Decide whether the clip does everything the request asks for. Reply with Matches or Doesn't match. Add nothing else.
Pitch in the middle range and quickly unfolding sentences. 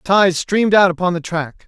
Matches